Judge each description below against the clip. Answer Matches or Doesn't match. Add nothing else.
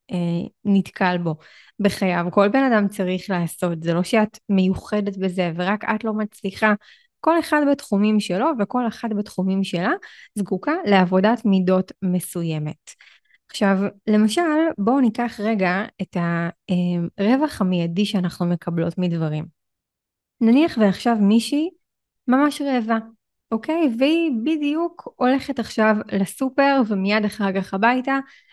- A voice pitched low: Doesn't match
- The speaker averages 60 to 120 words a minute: Matches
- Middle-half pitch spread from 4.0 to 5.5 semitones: Matches